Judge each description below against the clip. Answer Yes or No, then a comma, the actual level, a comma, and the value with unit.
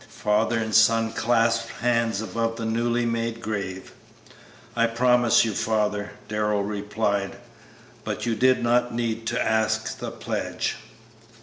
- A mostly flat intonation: Yes, narrow, 1.6 semitones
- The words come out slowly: Yes, slow, 130 wpm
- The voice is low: Yes, low, 115 Hz